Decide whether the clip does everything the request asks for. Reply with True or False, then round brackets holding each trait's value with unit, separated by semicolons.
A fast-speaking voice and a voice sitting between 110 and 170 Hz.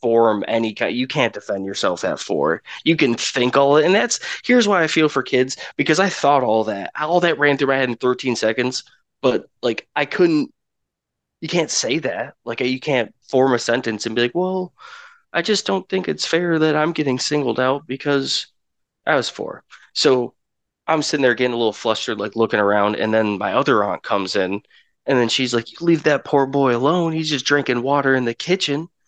True (215 wpm; 135 Hz)